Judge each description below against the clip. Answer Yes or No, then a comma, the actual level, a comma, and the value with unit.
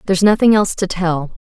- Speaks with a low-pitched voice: No, high, 190 Hz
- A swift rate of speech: Yes, fast, 210 wpm